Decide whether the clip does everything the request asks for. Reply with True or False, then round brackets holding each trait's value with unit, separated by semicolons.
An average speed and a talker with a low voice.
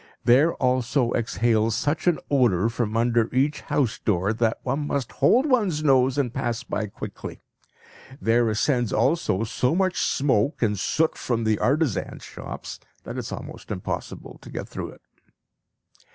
True (155 wpm; 120 Hz)